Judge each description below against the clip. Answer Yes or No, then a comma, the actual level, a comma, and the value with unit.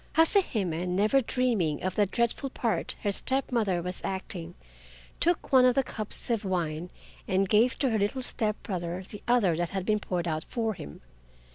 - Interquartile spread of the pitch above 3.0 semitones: Yes, average, 5.0 semitones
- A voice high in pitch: Yes, high, 205 Hz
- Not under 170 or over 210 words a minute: Yes, average, 185 wpm